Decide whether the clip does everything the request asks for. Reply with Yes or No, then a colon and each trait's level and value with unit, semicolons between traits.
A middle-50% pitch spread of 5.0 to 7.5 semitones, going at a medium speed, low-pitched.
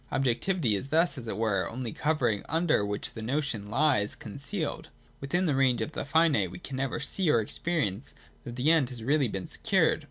No: wide, 5.6 semitones; fast, 210 wpm; low, 130 Hz